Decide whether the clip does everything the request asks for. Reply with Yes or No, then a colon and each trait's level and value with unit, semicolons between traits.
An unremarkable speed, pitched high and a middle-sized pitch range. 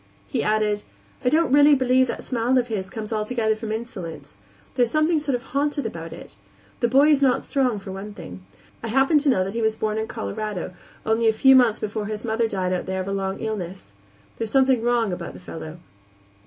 No: fast, 220 wpm; high, 220 Hz; average, 4.5 semitones